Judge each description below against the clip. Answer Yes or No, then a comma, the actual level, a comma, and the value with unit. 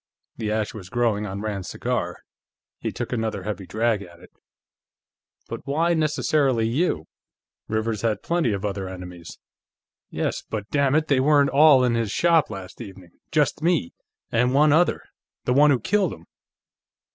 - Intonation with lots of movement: Yes, wide, 6.3 semitones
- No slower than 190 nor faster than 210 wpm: No, average, 155 wpm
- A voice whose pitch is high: No, low, 115 Hz